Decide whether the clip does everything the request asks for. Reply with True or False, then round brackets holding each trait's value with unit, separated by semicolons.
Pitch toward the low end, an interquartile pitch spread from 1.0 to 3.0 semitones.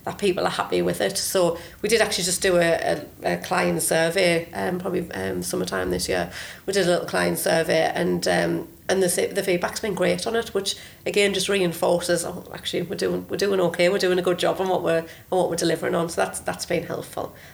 False (175 Hz; 2.5 semitones)